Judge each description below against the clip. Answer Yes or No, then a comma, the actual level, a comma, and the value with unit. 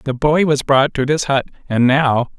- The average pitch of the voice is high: No, medium, 140 Hz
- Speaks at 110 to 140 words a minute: No, fast, 225 wpm